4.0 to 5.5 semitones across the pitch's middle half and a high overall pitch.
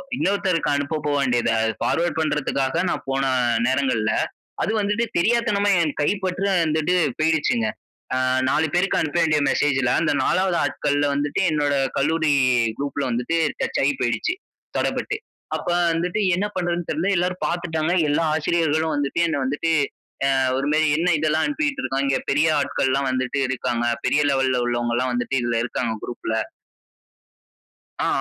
No: average, 4.3 semitones; medium, 150 Hz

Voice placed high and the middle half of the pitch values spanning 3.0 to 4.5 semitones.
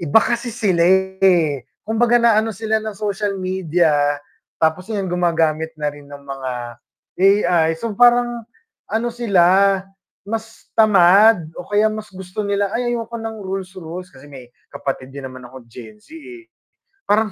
No: high, 195 Hz; average, 4.9 semitones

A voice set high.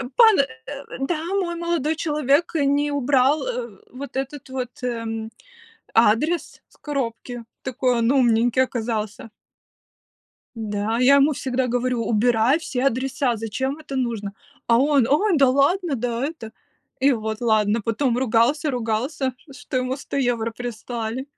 Yes: very high, 255 Hz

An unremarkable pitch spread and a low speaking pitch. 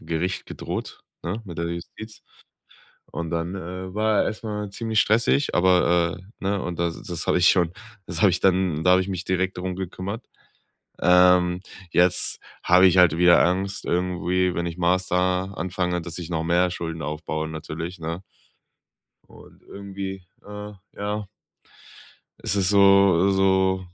No: narrow, 2.0 semitones; very low, 90 Hz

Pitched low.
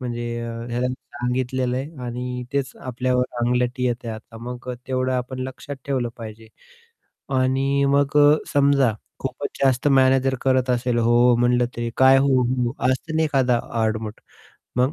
Yes: low, 125 Hz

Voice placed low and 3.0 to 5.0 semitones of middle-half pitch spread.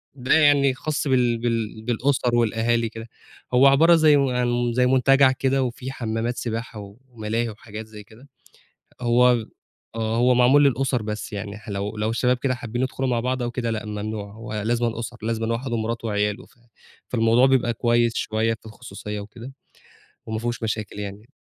No: low, 120 Hz; narrow, 2.4 semitones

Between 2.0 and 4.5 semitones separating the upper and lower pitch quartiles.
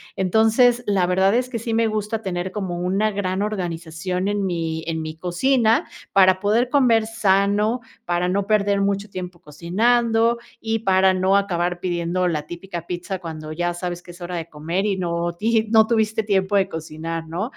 Yes: average, 3.7 semitones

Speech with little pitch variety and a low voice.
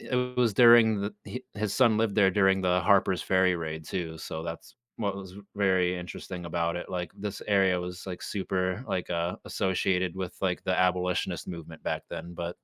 Yes: narrow, 2.2 semitones; very low, 95 Hz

